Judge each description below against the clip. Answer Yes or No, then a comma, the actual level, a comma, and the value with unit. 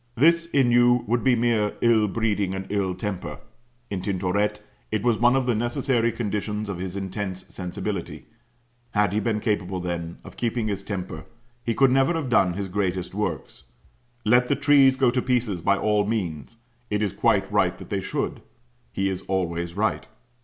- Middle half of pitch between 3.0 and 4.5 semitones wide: Yes, average, 4.1 semitones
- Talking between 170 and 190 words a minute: Yes, average, 175 wpm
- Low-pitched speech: Yes, low, 105 Hz